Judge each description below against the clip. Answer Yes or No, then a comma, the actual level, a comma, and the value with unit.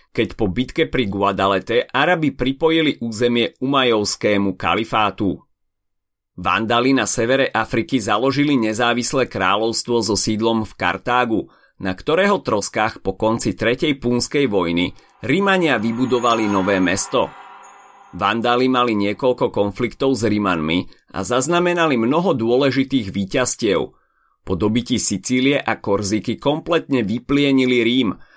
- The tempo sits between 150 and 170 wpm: No, slow, 110 wpm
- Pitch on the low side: Yes, low, 115 Hz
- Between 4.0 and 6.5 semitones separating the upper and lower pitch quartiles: Yes, average, 4.4 semitones